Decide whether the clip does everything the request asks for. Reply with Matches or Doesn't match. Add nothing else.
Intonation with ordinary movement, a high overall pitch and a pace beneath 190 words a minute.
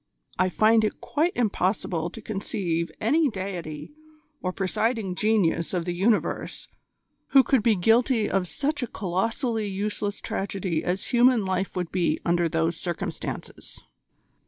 Matches